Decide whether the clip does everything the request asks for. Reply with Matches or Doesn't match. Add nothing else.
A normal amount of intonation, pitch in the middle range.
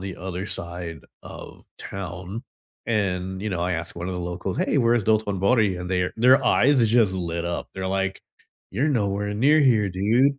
Doesn't match